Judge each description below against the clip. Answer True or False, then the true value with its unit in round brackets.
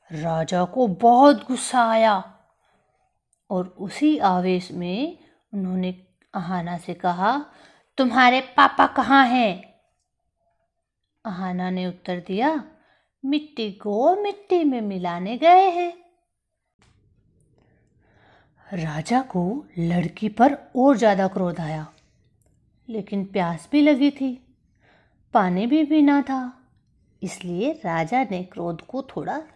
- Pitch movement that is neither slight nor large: False (7.2 semitones)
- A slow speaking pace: True (105 wpm)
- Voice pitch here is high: True (215 Hz)